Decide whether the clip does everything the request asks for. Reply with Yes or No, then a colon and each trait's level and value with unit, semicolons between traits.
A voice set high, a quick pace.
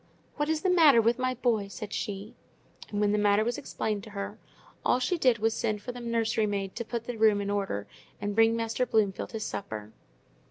Yes: high, 220 Hz; fast, 225 wpm